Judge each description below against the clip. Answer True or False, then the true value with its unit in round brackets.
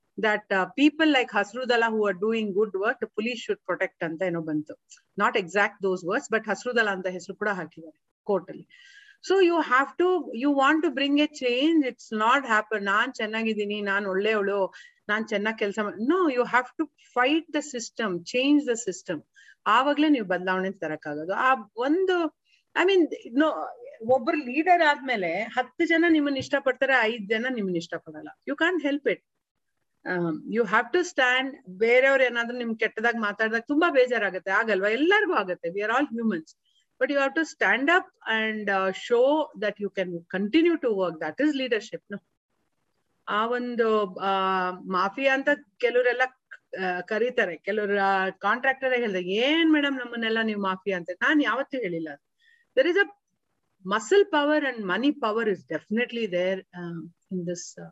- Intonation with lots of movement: True (6.2 semitones)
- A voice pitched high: True (230 Hz)